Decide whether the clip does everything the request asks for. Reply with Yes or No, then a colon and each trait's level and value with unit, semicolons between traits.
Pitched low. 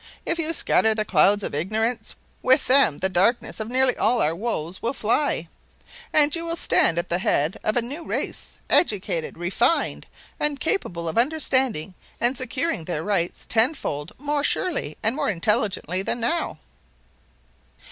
No: high, 225 Hz